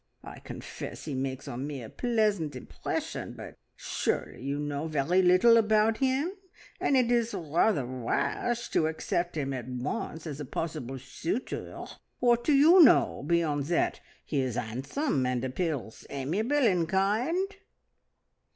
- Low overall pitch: No, medium, 165 Hz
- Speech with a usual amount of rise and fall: No, wide, 9.0 semitones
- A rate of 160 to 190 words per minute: No, average, 145 wpm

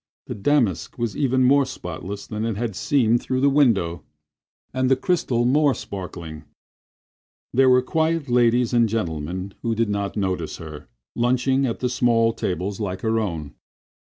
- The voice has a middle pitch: No, low, 115 Hz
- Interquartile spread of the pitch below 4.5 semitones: No, average, 5.1 semitones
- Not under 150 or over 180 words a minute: Yes, average, 155 wpm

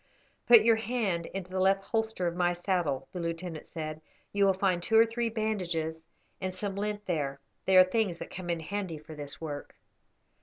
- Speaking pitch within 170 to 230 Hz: Yes, medium, 185 Hz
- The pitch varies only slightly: No, average, 3.8 semitones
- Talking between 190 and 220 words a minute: Yes, average, 195 wpm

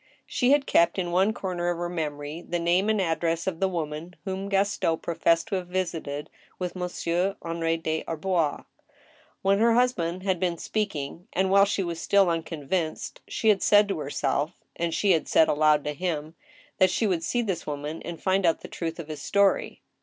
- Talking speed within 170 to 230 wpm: Yes, average, 195 wpm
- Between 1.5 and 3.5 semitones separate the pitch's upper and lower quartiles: Yes, average, 2.9 semitones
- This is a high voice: No, medium, 175 Hz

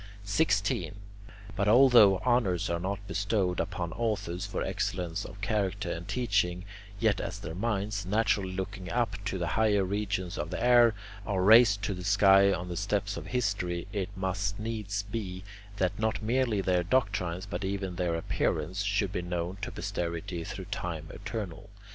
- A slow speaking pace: No, average, 165 wpm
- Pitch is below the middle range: Yes, low, 100 Hz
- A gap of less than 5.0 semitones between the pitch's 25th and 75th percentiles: Yes, narrow, 2.5 semitones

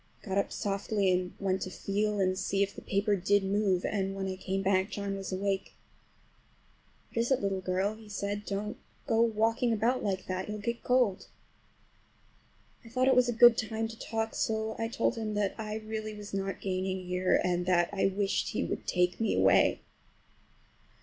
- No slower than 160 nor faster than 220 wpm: Yes, average, 190 wpm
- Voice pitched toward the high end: Yes, high, 200 Hz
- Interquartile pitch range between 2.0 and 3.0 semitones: Yes, narrow, 2.5 semitones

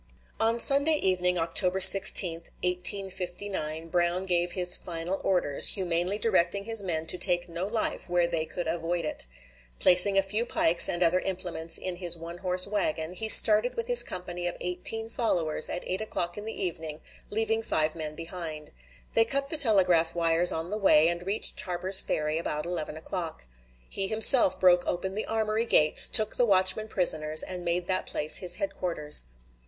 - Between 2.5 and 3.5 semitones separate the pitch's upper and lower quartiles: Yes, average, 2.9 semitones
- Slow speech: No, average, 175 wpm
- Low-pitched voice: No, medium, 180 Hz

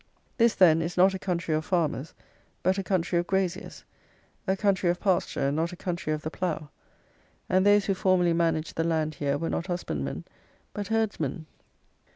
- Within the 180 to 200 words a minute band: Yes, average, 185 wpm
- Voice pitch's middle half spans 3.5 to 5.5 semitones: No, average, 3.1 semitones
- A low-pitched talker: No, medium, 175 Hz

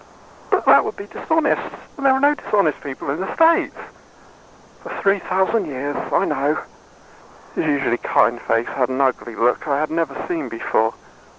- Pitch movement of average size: No, wide, 7.3 semitones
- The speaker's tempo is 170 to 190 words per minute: Yes, average, 175 wpm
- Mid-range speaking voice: Yes, medium, 150 Hz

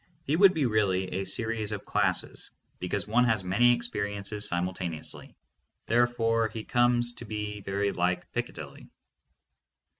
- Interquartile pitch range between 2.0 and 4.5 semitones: Yes, average, 3.7 semitones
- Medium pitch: No, low, 105 Hz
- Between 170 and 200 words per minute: No, average, 140 wpm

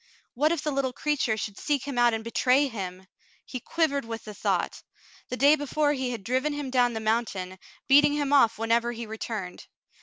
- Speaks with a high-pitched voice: Yes, high, 245 Hz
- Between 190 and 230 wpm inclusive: Yes, average, 200 wpm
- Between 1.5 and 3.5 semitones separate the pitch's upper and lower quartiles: No, average, 4.3 semitones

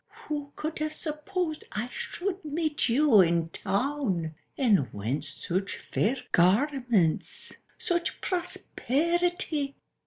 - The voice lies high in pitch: Yes, very high, 280 Hz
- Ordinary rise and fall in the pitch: No, wide, 8.4 semitones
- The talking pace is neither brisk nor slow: No, slow, 105 wpm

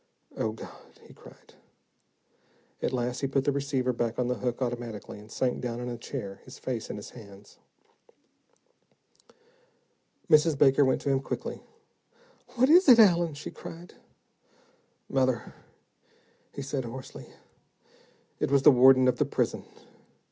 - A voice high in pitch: No, low, 130 Hz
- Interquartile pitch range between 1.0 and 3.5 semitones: Yes, average, 2.8 semitones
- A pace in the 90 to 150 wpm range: Yes, average, 145 wpm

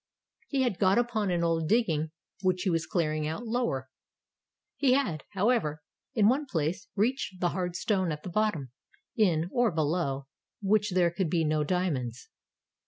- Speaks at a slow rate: No, average, 165 wpm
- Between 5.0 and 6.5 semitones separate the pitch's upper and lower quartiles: Yes, wide, 5.4 semitones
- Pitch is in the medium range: Yes, medium, 180 Hz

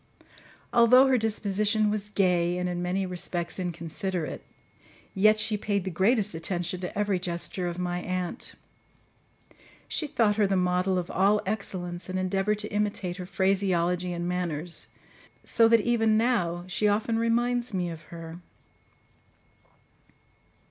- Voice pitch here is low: No, high, 190 Hz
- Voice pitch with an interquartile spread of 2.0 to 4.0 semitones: Yes, average, 3.1 semitones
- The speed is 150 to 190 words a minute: No, average, 140 wpm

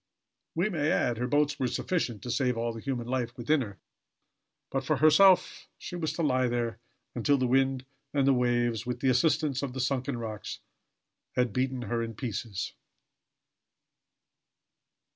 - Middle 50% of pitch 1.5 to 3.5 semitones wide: Yes, average, 2.8 semitones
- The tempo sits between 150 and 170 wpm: Yes, average, 160 wpm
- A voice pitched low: Yes, low, 125 Hz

